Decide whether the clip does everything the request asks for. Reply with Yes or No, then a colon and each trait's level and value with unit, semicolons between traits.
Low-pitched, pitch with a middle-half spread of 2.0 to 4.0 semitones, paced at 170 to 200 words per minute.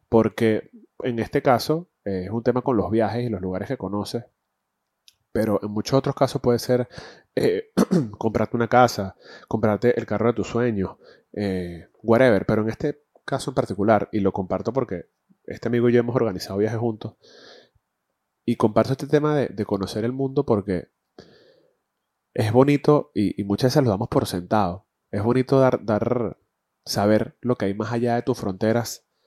Yes: low, 115 Hz; average, 3.6 semitones; average, 175 wpm